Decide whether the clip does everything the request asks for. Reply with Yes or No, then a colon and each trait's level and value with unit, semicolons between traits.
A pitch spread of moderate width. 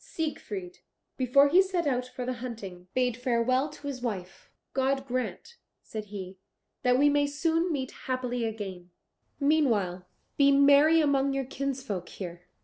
Yes: average, 4.0 semitones